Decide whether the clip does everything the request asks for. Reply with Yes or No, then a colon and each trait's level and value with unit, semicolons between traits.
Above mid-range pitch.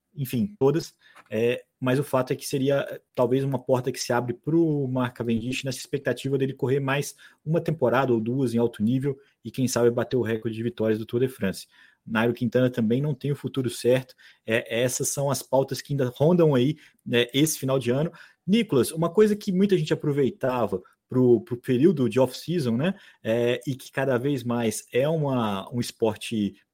No: low, 130 Hz